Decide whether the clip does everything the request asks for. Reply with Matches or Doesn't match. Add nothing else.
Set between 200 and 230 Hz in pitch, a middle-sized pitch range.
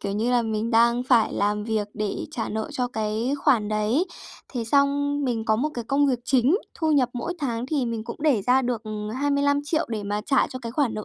Doesn't match